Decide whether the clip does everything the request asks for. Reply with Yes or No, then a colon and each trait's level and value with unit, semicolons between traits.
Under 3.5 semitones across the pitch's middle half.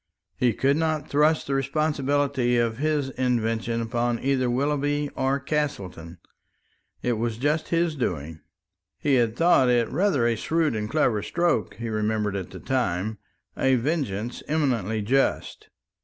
No: average, 4.5 semitones